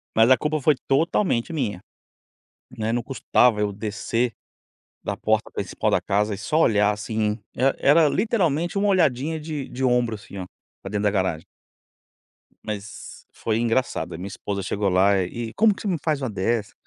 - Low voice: Yes, low, 115 Hz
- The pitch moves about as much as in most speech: No, wide, 6.3 semitones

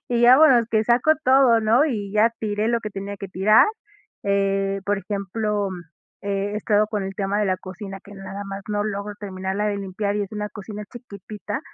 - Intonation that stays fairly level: Yes, narrow, 1.7 semitones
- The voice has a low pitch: No, high, 205 Hz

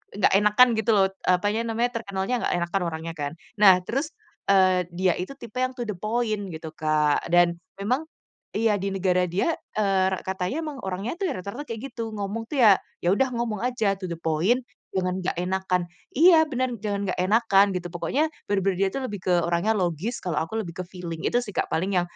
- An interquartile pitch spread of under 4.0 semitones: No, average, 4.3 semitones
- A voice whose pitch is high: Yes, high, 195 Hz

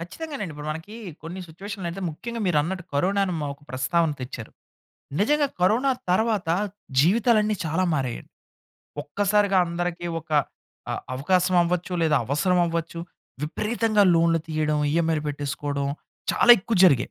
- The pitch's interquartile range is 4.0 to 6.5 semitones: Yes, average, 4.7 semitones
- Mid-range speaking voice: Yes, medium, 175 Hz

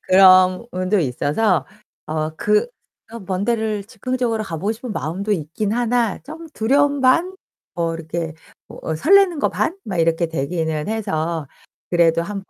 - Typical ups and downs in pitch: No, wide, 5.7 semitones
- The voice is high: Yes, high, 195 Hz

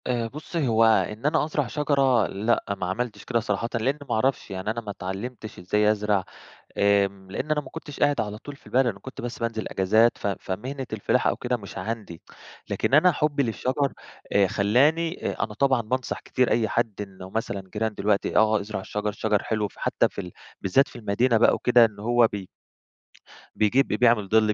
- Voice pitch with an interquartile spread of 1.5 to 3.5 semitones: No, average, 3.9 semitones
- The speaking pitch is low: Yes, low, 110 Hz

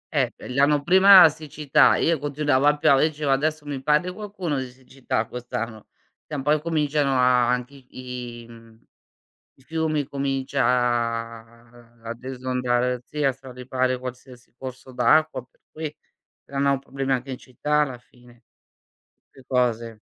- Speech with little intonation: No, average, 3.1 semitones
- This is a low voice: Yes, low, 130 Hz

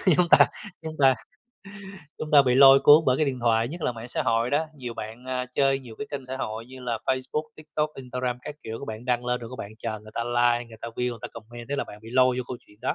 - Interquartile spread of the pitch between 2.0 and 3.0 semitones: Yes, average, 2.7 semitones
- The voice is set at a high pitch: No, low, 125 Hz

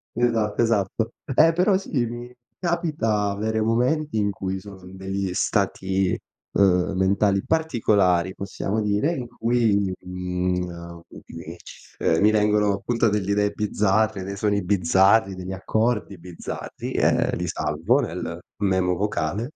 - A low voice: Yes, low, 100 Hz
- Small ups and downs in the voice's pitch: No, average, 3.2 semitones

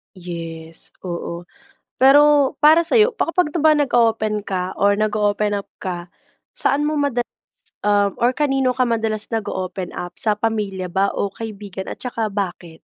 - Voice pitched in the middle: No, high, 215 Hz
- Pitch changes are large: Yes, wide, 5.9 semitones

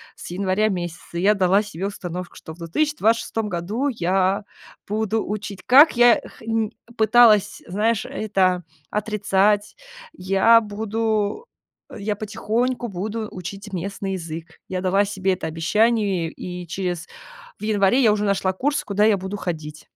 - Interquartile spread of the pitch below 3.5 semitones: Yes, average, 2.9 semitones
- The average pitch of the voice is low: No, high, 200 Hz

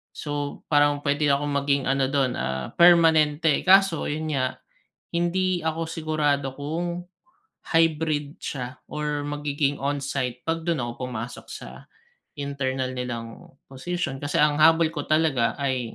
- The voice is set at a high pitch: No, medium, 145 Hz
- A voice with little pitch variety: No, average, 3.0 semitones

